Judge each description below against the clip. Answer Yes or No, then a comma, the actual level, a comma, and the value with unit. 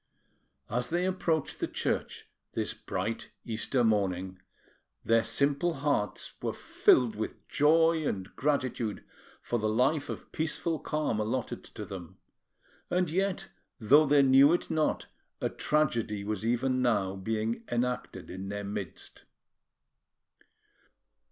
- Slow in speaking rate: Yes, slow, 125 wpm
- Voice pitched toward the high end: No, low, 125 Hz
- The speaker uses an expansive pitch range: Yes, wide, 5.9 semitones